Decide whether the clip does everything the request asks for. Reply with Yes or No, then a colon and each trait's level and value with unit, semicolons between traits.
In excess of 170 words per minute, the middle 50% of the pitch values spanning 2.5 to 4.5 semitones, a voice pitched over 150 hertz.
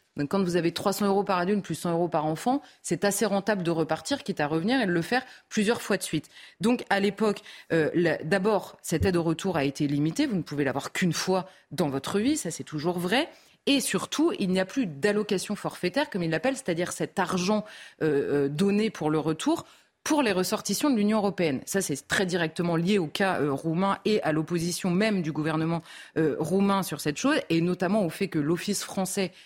Yes: fast, 220 wpm; average, 4.2 semitones; medium, 185 Hz